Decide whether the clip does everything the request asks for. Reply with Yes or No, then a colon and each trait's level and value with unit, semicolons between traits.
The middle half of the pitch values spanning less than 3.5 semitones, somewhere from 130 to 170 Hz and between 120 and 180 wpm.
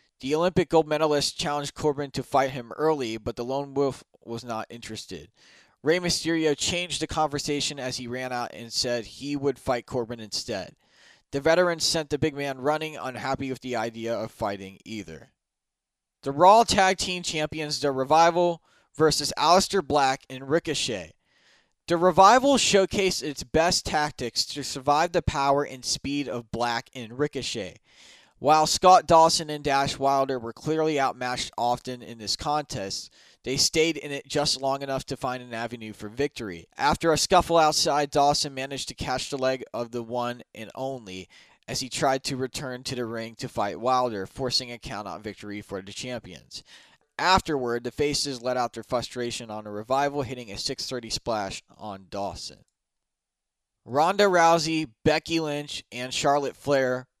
No: average, 4.1 semitones; low, 135 Hz; average, 165 wpm